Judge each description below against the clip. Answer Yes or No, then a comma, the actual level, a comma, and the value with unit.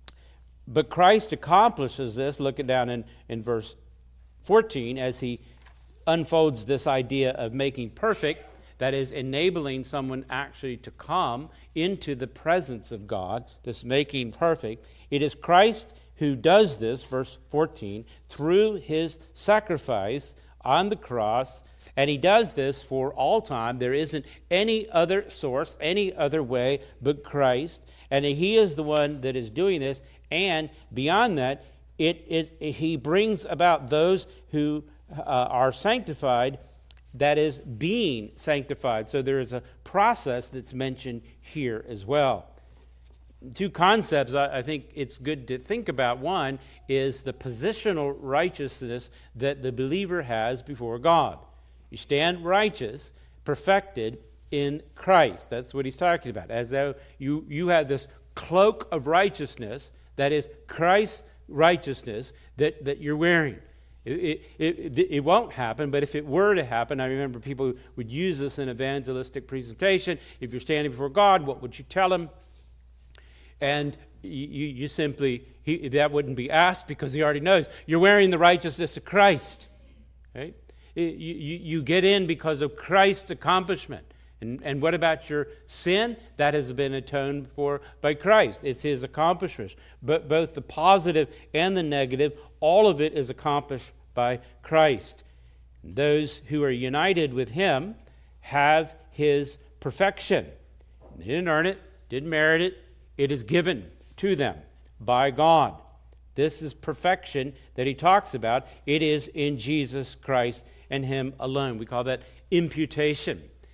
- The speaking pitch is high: No, medium, 140 Hz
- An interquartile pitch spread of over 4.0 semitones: Yes, average, 4.4 semitones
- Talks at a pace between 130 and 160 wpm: Yes, average, 150 wpm